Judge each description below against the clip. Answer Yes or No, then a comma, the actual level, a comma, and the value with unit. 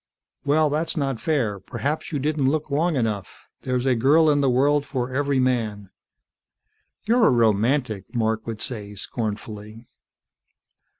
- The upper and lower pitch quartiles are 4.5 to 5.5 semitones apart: Yes, average, 4.8 semitones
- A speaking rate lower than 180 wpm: Yes, average, 140 wpm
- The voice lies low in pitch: Yes, low, 130 Hz